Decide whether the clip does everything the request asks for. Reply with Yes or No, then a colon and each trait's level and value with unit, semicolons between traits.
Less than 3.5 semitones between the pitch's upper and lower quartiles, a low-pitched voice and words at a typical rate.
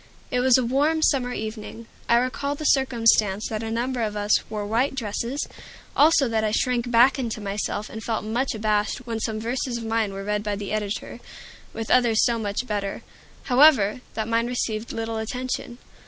No: average, 2.8 semitones; high, 230 Hz; average, 185 wpm